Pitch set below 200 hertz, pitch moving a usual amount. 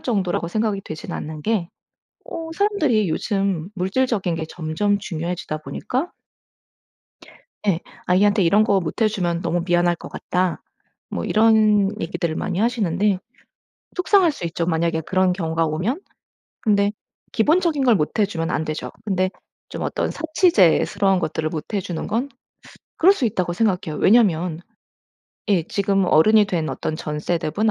Yes: high, 190 Hz; average, 4.5 semitones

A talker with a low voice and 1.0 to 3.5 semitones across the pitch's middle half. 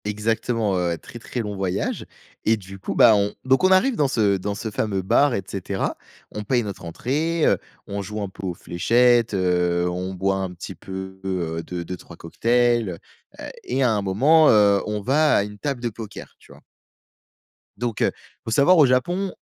No: low, 105 Hz; average, 4.3 semitones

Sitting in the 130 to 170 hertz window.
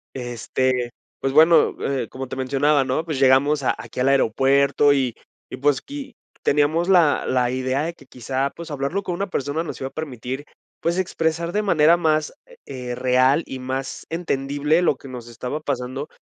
Yes: medium, 140 Hz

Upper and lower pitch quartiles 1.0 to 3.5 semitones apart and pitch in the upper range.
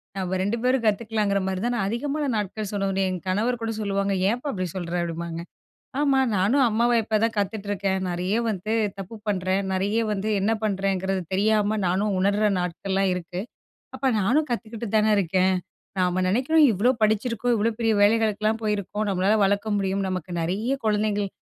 Yes: average, 2.8 semitones; high, 205 Hz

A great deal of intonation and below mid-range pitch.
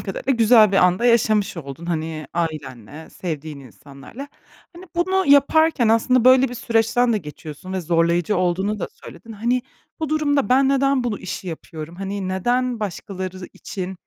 No: wide, 6.5 semitones; high, 205 Hz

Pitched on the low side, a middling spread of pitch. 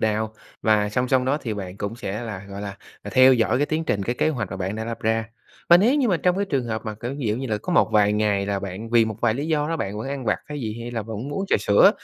Yes: low, 115 Hz; average, 4.4 semitones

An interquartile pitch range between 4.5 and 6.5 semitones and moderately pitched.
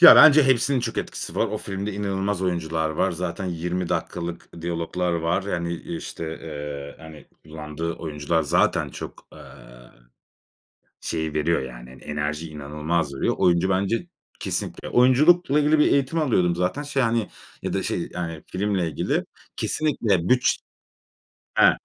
No: average, 5.3 semitones; very low, 85 Hz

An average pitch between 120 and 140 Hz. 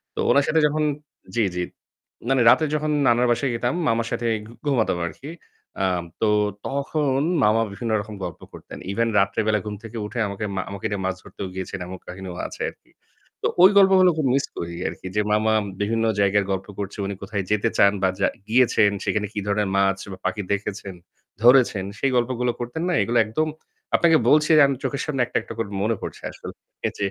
No: low, 110 Hz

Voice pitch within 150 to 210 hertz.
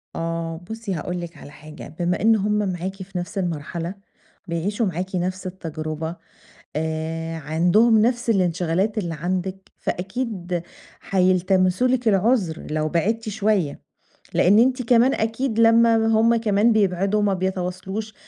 Yes: medium, 185 Hz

